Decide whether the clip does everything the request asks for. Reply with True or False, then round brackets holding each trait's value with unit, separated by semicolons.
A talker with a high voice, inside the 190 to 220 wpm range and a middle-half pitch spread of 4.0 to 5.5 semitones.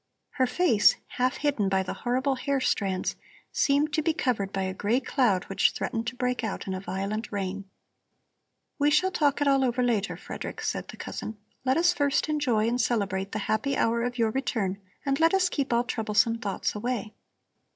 True (240 Hz; 195 wpm; 5.2 semitones)